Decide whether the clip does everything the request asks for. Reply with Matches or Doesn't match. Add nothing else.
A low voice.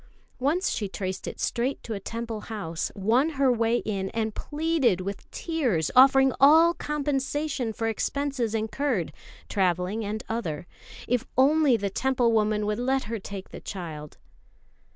Doesn't match